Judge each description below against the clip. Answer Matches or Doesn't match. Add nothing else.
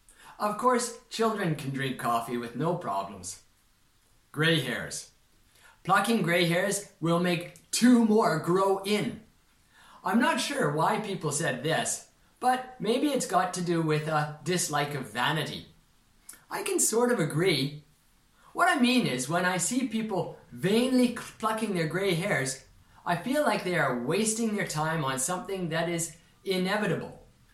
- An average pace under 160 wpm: Matches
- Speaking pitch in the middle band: Matches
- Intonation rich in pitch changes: Matches